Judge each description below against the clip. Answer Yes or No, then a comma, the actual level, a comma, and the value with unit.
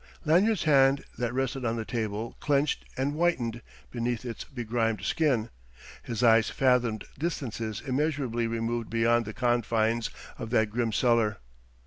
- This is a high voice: No, low, 120 Hz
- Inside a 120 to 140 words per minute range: Yes, slow, 135 wpm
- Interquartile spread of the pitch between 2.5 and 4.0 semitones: Yes, average, 2.9 semitones